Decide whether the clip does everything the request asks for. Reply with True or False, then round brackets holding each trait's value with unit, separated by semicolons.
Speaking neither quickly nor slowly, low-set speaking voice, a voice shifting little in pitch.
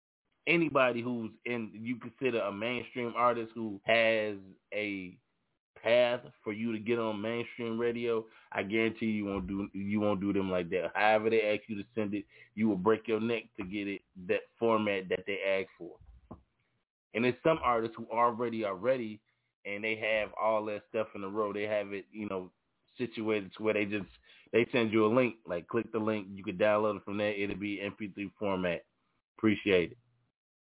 True (195 wpm; 110 Hz; 2.3 semitones)